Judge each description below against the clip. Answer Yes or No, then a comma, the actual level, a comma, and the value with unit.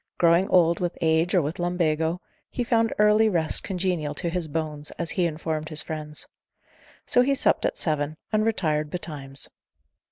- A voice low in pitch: No, medium, 170 Hz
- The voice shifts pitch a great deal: No, average, 3.1 semitones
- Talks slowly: No, average, 165 wpm